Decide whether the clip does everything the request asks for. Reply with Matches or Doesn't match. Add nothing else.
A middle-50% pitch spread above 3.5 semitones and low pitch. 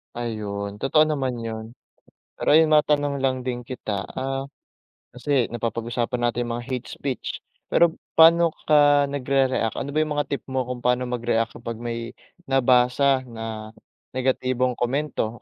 Doesn't match